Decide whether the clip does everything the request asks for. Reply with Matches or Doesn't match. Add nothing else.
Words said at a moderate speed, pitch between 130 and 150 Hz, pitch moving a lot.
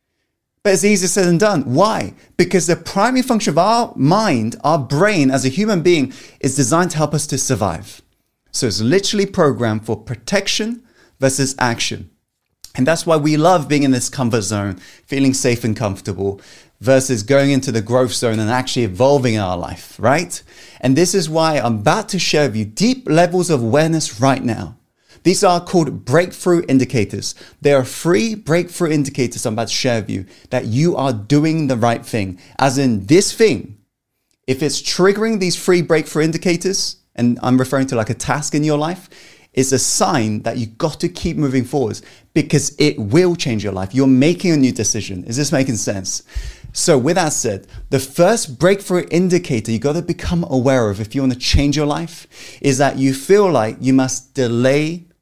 Matches